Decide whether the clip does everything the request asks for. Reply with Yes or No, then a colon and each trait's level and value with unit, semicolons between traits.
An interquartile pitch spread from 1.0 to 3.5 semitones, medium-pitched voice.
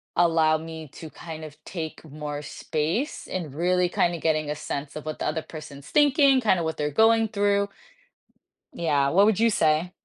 No: average, 4.5 semitones; medium, 160 Hz